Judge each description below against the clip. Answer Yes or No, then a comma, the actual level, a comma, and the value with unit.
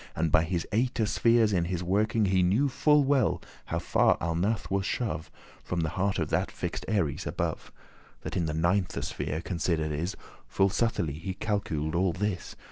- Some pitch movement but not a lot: Yes, average, 4.4 semitones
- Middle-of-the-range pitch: No, very low, 95 Hz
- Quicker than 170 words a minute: Yes, average, 185 wpm